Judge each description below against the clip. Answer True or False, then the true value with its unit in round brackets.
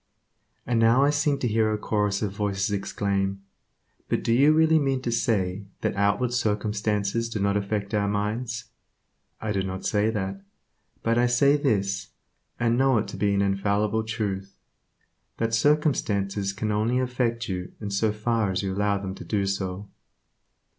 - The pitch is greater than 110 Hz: False (105 Hz)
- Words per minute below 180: True (170 wpm)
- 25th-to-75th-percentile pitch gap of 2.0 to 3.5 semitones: True (2.8 semitones)